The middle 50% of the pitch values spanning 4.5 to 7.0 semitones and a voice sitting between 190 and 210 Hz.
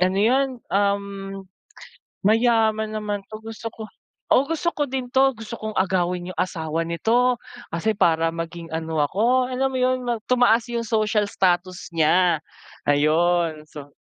Yes: wide, 5.6 semitones; high, 205 Hz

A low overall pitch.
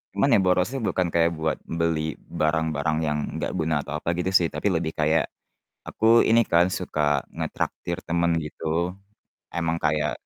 Yes: very low, 80 Hz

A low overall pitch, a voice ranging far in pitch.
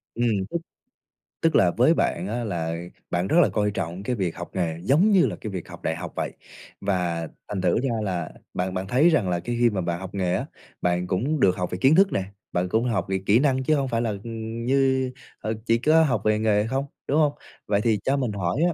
Yes: low, 110 Hz; wide, 6.4 semitones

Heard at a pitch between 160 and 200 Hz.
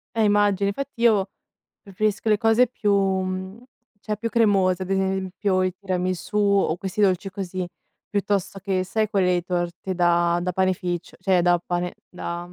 Yes: high, 190 Hz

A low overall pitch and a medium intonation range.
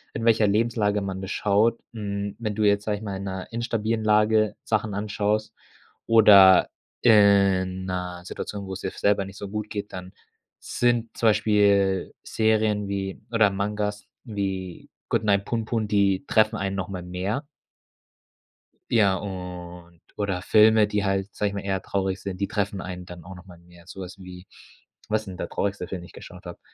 No: low, 100 Hz; narrow, 2.1 semitones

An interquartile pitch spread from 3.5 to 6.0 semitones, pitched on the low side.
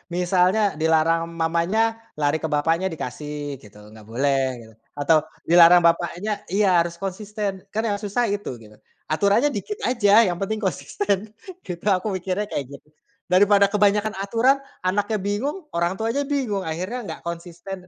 No: average, 3.8 semitones; medium, 185 Hz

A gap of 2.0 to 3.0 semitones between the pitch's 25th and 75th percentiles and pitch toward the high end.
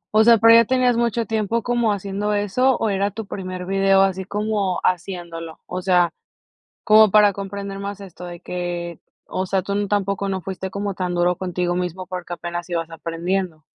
Yes: narrow, 2.4 semitones; high, 195 Hz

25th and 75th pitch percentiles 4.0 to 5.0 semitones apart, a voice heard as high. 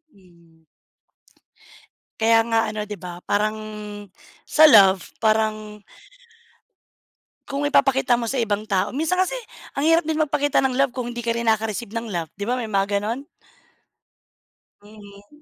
Yes: average, 4.6 semitones; high, 220 Hz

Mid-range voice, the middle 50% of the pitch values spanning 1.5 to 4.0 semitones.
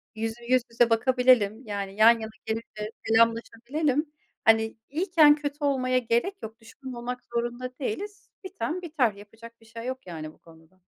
No: high, 235 Hz; average, 2.9 semitones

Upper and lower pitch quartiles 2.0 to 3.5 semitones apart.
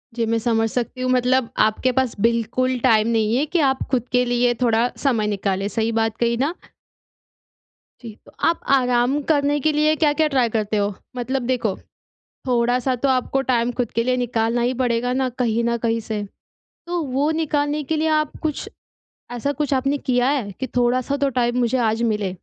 Yes: average, 2.8 semitones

